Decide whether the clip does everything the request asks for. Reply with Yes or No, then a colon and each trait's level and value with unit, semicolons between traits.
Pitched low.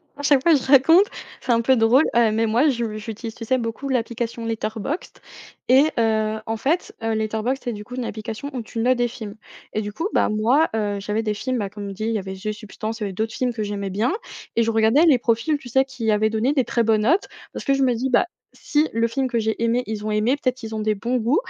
No: high, 230 Hz